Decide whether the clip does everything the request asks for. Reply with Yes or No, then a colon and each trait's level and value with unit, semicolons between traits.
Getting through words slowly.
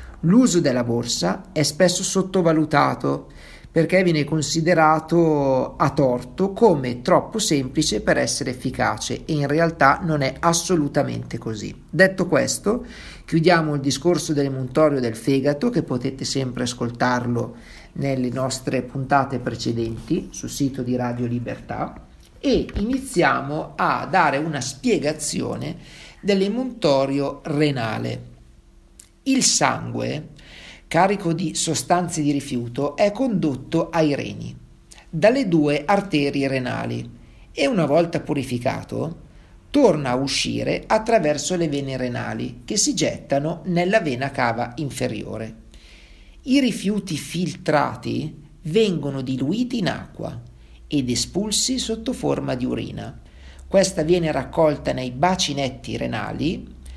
Yes: slow, 110 wpm